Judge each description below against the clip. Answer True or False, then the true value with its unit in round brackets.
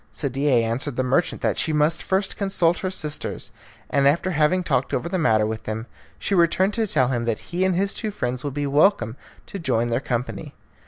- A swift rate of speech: True (210 wpm)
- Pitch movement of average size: False (6.8 semitones)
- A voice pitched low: False (150 Hz)